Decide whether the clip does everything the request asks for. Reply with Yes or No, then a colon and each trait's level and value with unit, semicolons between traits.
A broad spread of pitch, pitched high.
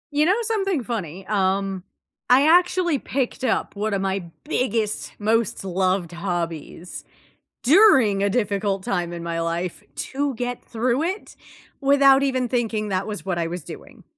Yes: wide, 6.1 semitones; high, 210 Hz